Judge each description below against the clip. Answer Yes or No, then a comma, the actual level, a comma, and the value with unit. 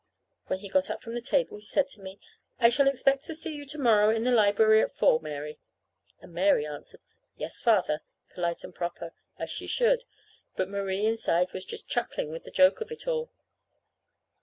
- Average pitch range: No, wide, 6.9 semitones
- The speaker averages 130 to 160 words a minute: No, average, 200 wpm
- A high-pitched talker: Yes, high, 220 Hz